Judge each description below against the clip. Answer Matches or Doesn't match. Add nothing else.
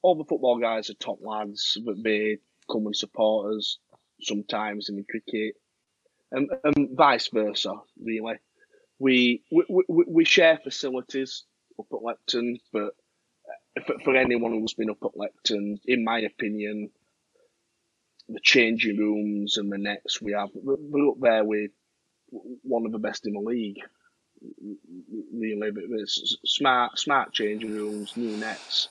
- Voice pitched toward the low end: Matches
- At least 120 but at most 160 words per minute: Matches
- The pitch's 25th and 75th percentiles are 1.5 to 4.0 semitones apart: Doesn't match